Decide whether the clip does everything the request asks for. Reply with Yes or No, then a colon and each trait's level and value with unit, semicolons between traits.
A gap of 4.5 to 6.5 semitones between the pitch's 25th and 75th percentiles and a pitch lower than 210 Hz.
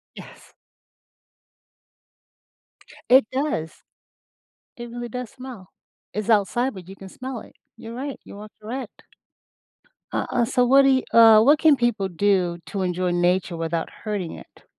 No: average, 5.2 semitones; high, 220 Hz